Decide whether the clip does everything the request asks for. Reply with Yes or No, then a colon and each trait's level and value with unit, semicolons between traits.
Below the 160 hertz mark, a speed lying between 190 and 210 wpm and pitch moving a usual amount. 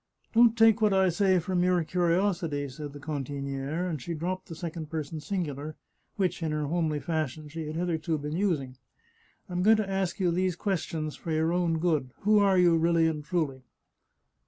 No: medium, 165 Hz; average, 195 wpm; average, 3.2 semitones